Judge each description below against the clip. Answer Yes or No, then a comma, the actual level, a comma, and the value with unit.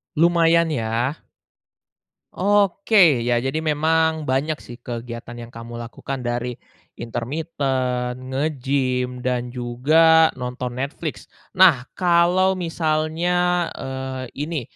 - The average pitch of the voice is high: No, low, 135 Hz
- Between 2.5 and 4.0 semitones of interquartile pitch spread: No, average, 4.8 semitones